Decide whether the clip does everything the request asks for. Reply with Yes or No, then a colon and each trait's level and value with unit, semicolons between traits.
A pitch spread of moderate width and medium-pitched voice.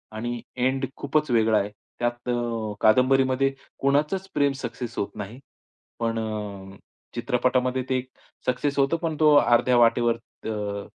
No: average, 3.0 semitones; low, 125 Hz